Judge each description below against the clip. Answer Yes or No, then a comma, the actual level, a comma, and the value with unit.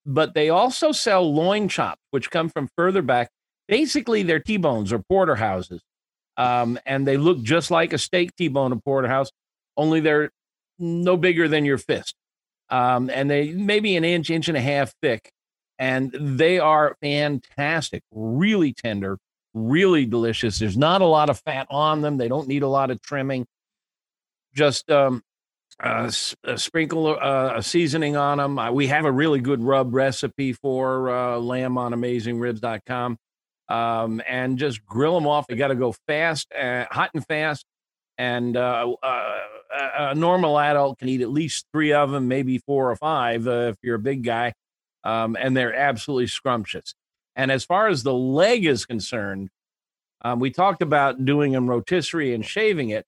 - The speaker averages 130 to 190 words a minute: Yes, average, 175 wpm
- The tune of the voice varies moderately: Yes, average, 4.1 semitones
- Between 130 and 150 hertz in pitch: Yes, medium, 140 Hz